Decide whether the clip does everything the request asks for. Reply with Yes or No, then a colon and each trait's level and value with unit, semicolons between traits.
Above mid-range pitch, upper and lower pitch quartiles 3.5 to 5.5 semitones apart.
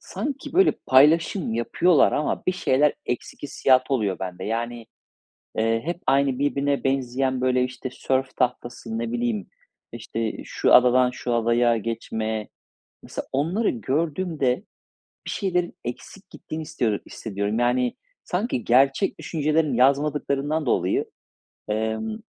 No: low, 130 Hz; average, 4.9 semitones